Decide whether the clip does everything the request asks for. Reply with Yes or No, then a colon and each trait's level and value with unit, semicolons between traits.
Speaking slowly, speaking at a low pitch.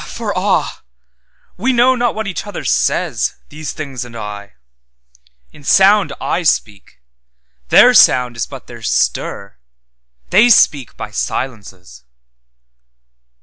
Yes: slow, 110 wpm; low, 125 Hz